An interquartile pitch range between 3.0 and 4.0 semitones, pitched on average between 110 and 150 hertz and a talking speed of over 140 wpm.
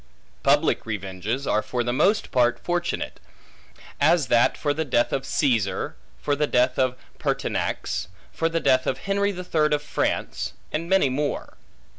No: average, 5.1 semitones; medium, 140 Hz; average, 160 wpm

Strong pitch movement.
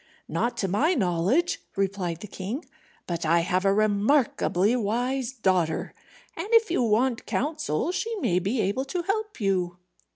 Yes: wide, 6.9 semitones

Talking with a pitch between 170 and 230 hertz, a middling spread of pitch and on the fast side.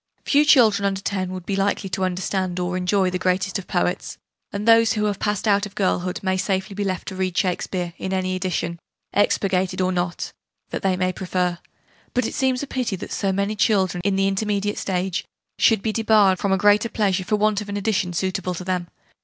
No: high, 190 Hz; narrow, 2.0 semitones; fast, 210 wpm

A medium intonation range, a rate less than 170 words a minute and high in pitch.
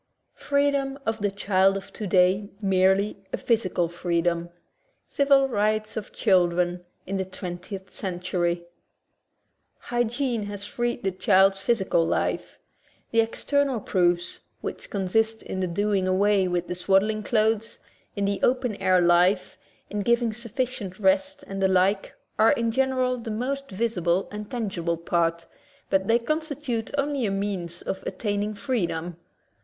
Yes: average, 4.1 semitones; average, 140 wpm; high, 205 Hz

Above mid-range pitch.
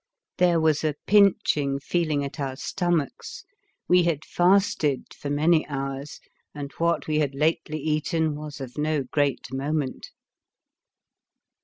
No: medium, 150 Hz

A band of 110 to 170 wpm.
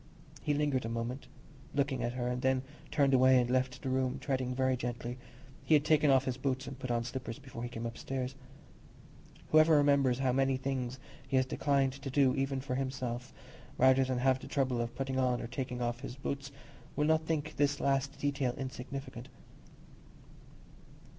No: average, 180 wpm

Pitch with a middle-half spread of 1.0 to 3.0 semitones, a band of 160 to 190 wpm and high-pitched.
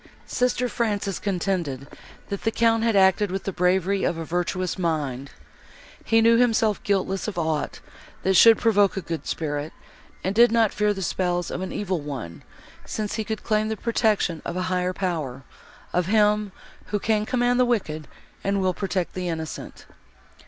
No: average, 3.8 semitones; average, 175 wpm; high, 195 Hz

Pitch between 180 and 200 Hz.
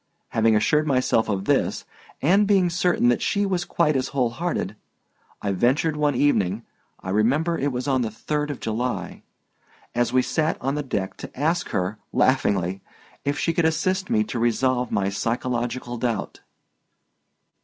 No: low, 130 Hz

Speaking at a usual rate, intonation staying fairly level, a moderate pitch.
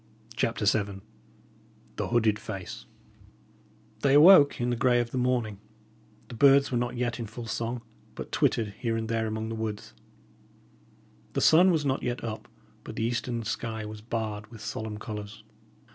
No: average, 165 wpm; narrow, 2.1 semitones; low, 115 Hz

